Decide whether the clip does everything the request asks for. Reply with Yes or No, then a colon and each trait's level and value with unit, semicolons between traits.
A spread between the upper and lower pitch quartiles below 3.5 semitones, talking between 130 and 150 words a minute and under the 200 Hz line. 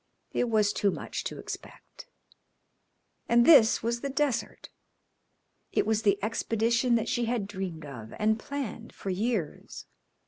No: average, 2.8 semitones; average, 140 wpm; high, 225 Hz